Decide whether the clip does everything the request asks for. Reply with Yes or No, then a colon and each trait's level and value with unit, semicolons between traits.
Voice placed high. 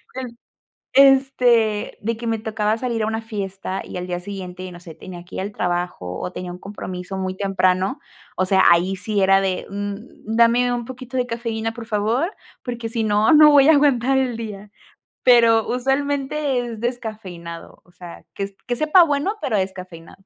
Yes: high, 220 Hz